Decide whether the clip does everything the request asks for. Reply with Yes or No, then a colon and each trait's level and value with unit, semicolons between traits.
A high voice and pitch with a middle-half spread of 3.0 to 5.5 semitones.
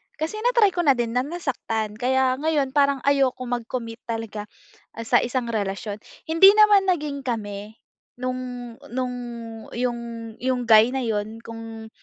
Yes: high, 245 Hz; average, 3.6 semitones